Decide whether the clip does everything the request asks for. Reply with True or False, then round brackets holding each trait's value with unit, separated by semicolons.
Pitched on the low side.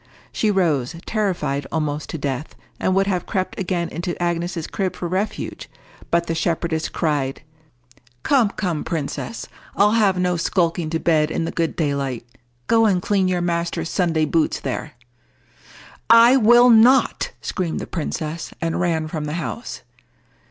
False (170 Hz)